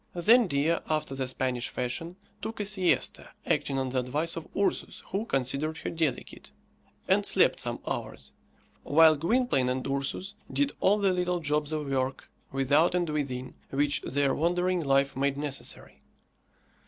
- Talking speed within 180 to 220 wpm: No, average, 155 wpm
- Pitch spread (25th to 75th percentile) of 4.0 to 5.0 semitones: Yes, average, 4.5 semitones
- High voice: No, medium, 150 Hz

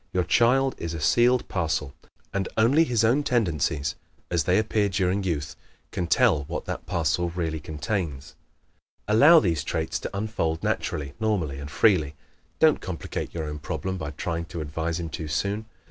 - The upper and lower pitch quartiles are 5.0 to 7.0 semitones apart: Yes, wide, 5.5 semitones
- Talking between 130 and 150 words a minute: No, average, 165 wpm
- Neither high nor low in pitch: No, very low, 85 Hz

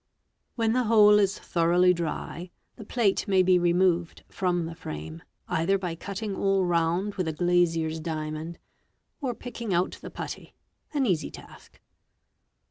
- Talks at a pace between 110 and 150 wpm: Yes, average, 140 wpm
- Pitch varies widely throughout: No, average, 3.3 semitones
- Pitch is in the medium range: Yes, medium, 180 Hz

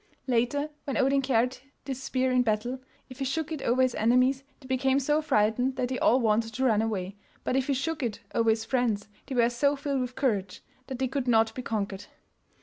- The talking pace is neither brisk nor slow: No, fast, 220 wpm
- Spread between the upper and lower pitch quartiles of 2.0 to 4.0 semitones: Yes, average, 3.0 semitones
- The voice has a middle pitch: No, very high, 255 Hz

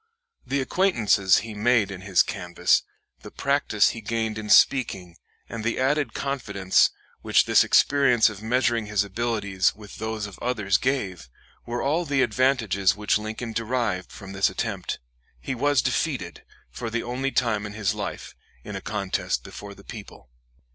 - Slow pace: No, average, 160 wpm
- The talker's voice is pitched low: Yes, low, 110 Hz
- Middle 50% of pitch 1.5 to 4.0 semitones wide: Yes, average, 3.7 semitones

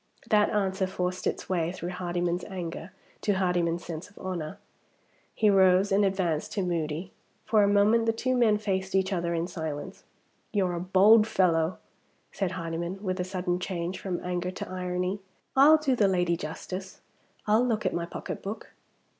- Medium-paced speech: Yes, average, 170 wpm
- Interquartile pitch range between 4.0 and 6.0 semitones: No, narrow, 2.6 semitones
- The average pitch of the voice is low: No, medium, 185 Hz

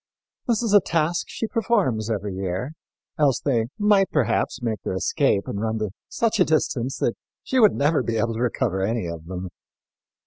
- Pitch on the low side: Yes, low, 120 Hz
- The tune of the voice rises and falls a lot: Yes, wide, 8.5 semitones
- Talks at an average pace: Yes, average, 185 wpm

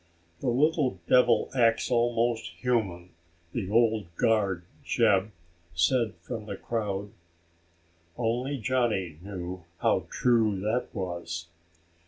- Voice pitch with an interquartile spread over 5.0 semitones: No, average, 4.0 semitones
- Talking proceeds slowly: Yes, slow, 105 wpm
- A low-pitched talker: Yes, low, 110 Hz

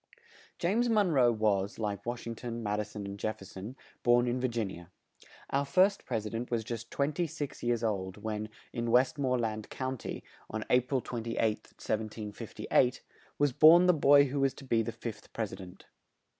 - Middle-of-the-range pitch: No, low, 115 Hz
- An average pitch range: Yes, average, 3.8 semitones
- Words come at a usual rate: No, fast, 210 wpm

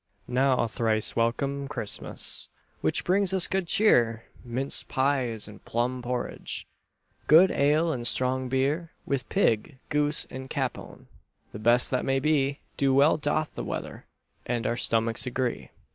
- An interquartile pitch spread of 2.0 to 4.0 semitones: Yes, average, 3.7 semitones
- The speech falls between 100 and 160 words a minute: Yes, average, 145 wpm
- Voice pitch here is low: Yes, low, 130 Hz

